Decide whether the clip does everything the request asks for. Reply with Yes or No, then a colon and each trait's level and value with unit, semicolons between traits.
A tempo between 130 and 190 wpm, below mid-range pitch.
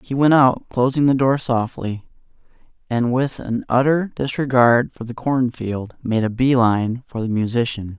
Yes: average, 175 wpm; low, 125 Hz